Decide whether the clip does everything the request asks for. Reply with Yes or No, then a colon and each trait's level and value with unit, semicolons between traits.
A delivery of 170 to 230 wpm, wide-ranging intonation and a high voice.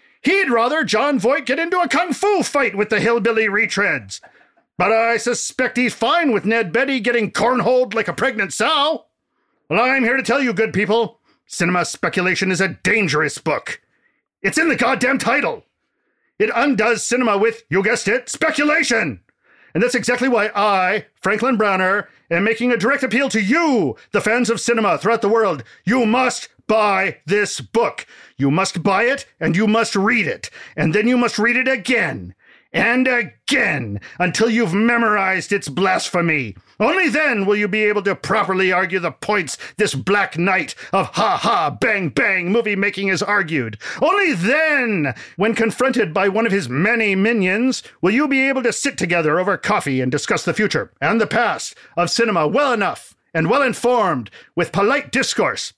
No: average, 175 wpm; average, 4.2 semitones; high, 225 Hz